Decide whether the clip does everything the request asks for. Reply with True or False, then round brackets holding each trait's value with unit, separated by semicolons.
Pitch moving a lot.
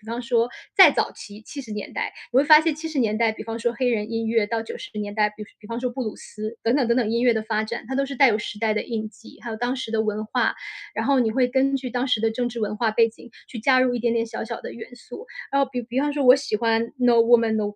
False (2.4 semitones)